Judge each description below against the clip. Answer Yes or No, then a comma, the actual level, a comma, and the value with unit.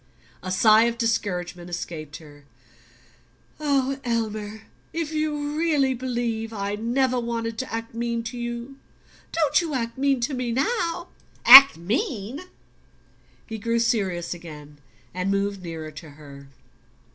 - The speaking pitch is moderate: No, high, 230 Hz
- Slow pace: Yes, slow, 130 wpm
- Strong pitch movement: Yes, wide, 6.0 semitones